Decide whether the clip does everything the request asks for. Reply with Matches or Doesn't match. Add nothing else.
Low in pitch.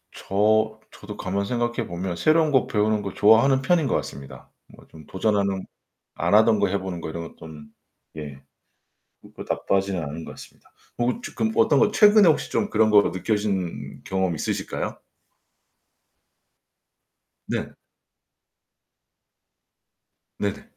Matches